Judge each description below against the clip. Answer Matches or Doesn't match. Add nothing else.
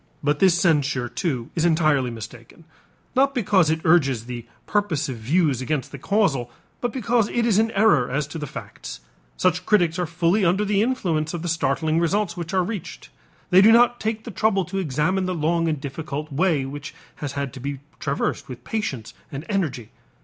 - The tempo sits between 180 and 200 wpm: Matches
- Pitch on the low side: Doesn't match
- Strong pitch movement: Matches